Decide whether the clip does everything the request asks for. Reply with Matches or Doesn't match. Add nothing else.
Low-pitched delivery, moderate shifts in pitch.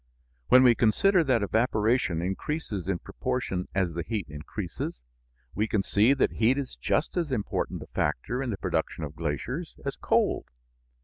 Doesn't match